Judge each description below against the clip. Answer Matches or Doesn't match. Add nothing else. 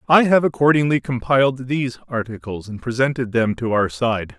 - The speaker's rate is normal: Matches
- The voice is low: Matches